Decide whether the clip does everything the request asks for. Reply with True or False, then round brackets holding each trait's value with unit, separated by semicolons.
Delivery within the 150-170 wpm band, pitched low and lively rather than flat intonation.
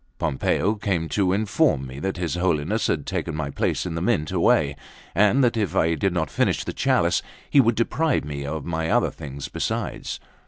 False (190 wpm; 85 Hz; 5.7 semitones)